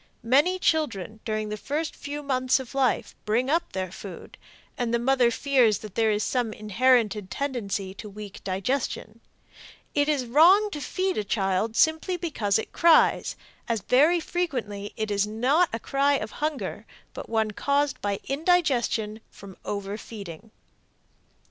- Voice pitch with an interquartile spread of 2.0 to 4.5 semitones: No, wide, 5.4 semitones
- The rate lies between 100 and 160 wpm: Yes, average, 150 wpm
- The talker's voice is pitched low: No, high, 235 Hz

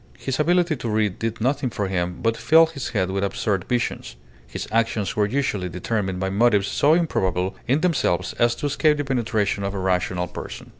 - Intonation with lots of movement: Yes, wide, 6.0 semitones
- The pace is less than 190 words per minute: No, average, 195 wpm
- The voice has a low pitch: Yes, low, 110 Hz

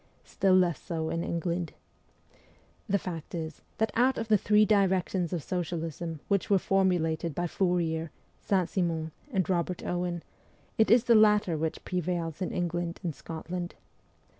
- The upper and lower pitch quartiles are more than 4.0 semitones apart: No, narrow, 2.6 semitones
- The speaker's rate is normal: Yes, average, 150 wpm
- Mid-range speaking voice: Yes, medium, 175 Hz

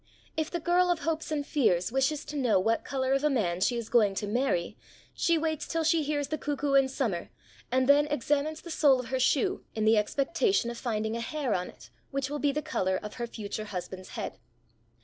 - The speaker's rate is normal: No, fast, 225 wpm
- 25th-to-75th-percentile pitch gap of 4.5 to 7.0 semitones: Yes, wide, 5.4 semitones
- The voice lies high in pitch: Yes, very high, 270 Hz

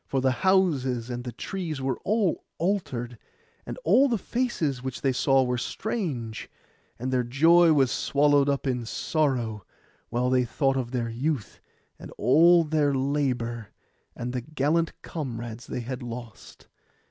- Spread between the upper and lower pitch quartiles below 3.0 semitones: No, average, 4.3 semitones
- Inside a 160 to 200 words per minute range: No, average, 150 wpm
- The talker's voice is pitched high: No, low, 135 Hz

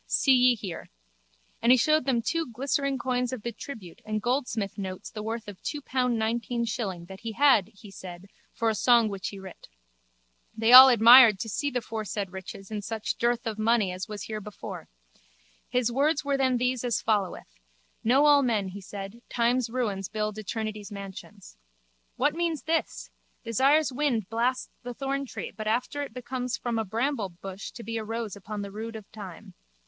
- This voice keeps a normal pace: Yes, average, 180 wpm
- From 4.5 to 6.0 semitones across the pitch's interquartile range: No, average, 3.6 semitones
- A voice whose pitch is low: No, high, 230 Hz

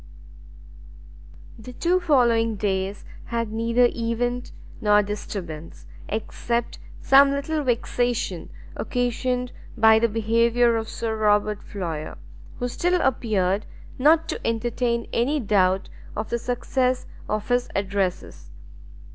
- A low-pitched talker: No, high, 230 Hz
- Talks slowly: Yes, slow, 110 wpm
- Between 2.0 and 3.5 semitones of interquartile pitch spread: Yes, average, 3.0 semitones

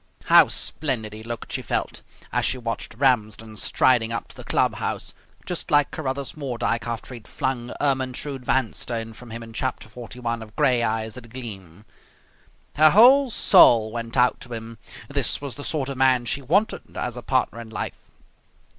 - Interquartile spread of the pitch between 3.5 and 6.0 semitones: No, average, 2.9 semitones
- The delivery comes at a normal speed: Yes, average, 180 wpm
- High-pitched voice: No, low, 120 Hz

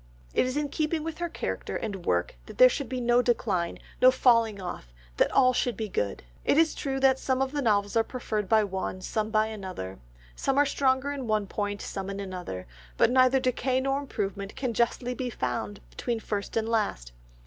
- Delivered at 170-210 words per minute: Yes, fast, 205 wpm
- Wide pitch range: No, average, 4.8 semitones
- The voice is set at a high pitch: Yes, high, 230 Hz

